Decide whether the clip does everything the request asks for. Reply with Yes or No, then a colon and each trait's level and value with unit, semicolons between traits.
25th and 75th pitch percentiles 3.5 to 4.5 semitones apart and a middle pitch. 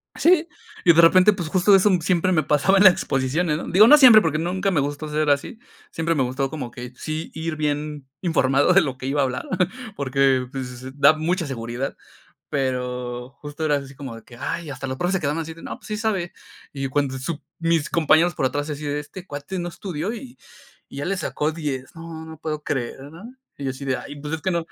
Yes: average, 4.1 semitones; medium, 150 Hz